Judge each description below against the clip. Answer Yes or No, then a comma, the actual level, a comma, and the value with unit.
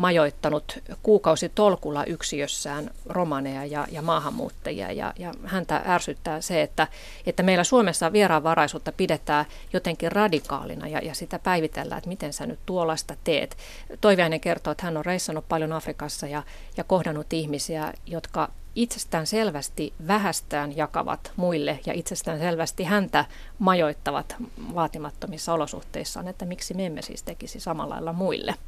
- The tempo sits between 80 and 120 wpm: No, average, 135 wpm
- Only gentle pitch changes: No, average, 3.2 semitones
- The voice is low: No, medium, 165 Hz